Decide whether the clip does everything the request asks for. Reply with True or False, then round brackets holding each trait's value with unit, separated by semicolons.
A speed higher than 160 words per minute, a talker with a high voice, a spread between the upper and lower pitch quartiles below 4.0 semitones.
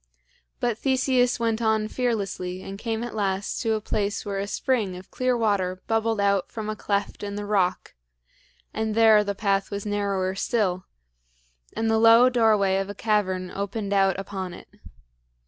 True (170 wpm; 205 Hz; 2.4 semitones)